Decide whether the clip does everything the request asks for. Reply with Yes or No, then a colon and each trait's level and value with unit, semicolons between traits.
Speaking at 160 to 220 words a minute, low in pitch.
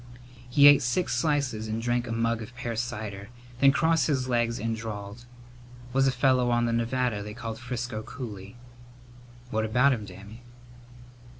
Yes: average, 165 wpm; low, 120 Hz